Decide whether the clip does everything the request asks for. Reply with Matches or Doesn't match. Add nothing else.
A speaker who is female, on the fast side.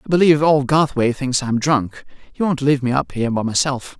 Doesn't match